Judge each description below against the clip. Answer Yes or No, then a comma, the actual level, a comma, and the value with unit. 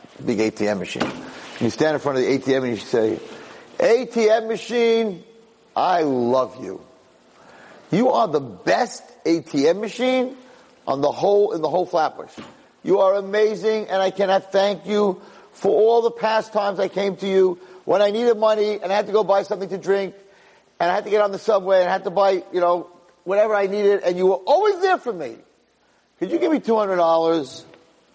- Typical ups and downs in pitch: Yes, average, 3.7 semitones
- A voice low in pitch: No, high, 195 Hz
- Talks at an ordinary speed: Yes, average, 195 wpm